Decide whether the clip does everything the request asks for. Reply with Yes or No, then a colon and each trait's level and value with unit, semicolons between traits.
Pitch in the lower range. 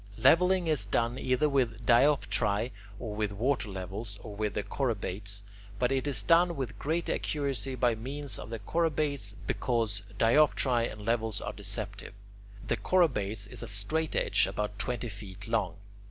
Yes: low, 115 Hz